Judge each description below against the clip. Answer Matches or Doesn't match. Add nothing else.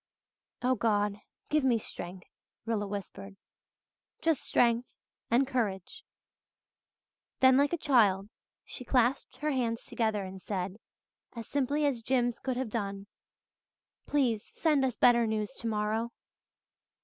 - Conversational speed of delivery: Doesn't match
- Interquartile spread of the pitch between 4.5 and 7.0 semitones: Doesn't match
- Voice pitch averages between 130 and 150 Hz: Doesn't match